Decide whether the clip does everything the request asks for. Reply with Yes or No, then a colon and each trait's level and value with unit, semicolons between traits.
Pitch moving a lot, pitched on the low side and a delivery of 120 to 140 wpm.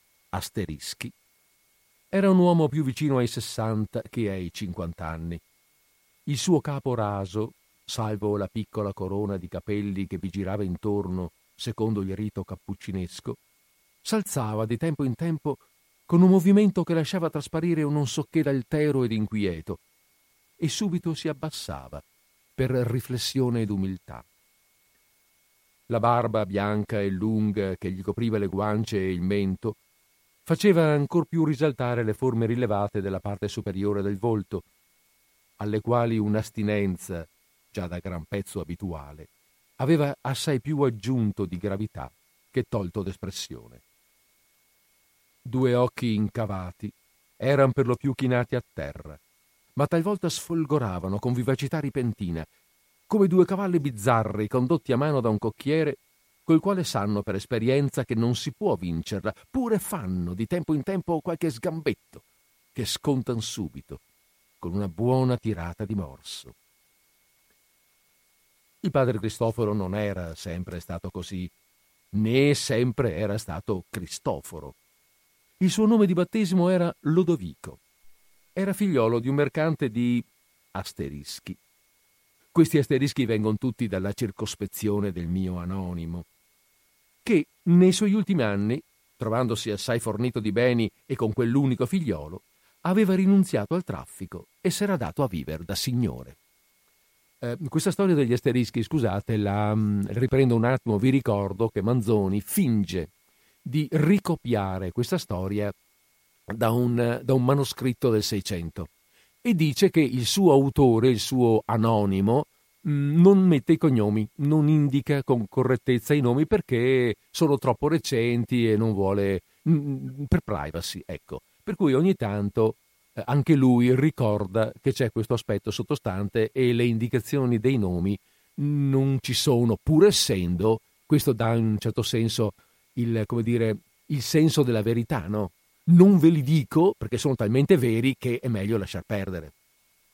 Yes: wide, 5.9 semitones; low, 115 Hz; average, 135 wpm